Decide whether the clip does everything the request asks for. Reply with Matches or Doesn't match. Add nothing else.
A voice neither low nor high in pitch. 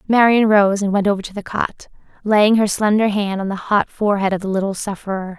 Doesn't match